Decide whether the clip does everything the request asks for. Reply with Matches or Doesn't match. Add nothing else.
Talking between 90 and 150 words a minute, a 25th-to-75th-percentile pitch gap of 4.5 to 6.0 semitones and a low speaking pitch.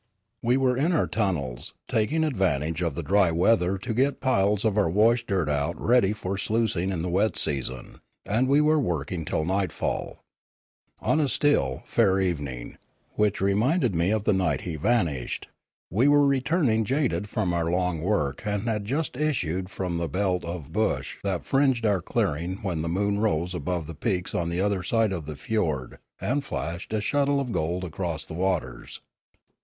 Doesn't match